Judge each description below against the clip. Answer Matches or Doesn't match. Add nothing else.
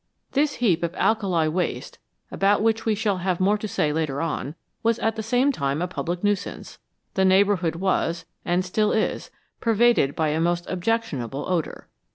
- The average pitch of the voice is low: Doesn't match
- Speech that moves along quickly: Doesn't match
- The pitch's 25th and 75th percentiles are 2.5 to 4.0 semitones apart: Doesn't match